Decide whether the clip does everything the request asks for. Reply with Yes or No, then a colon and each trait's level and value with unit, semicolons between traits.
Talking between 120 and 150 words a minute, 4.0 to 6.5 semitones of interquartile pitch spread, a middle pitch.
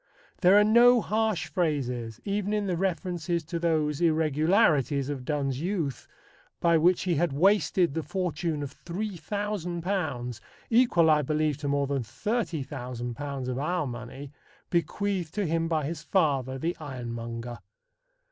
Yes: average, 140 wpm; average, 4.8 semitones; medium, 160 Hz